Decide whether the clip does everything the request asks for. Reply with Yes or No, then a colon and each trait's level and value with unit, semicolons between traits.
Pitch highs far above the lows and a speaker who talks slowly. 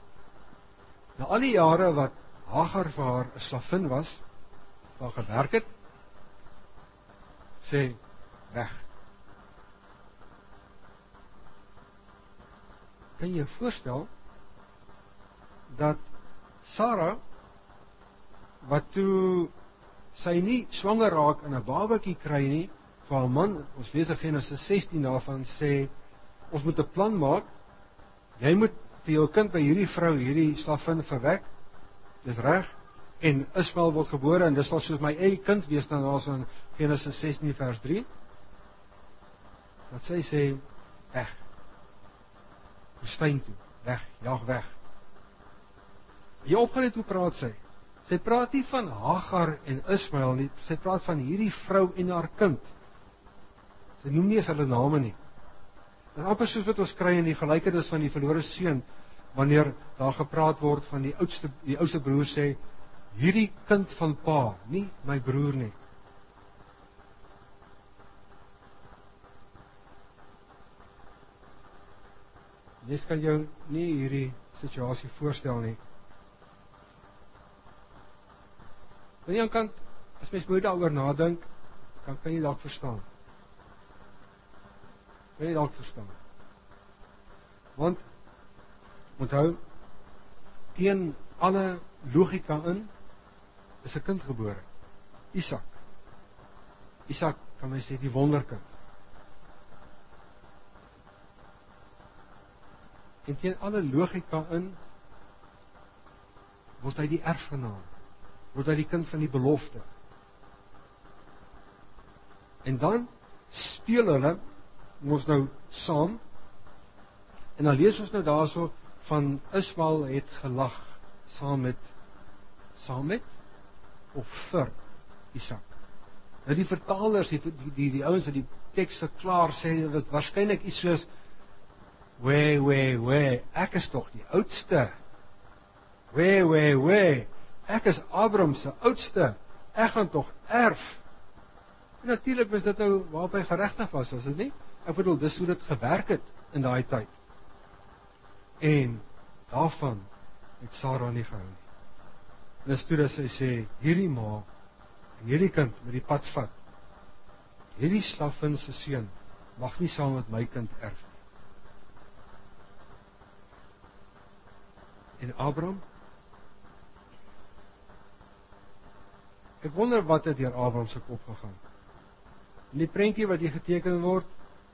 Yes: wide, 7.3 semitones; slow, 115 wpm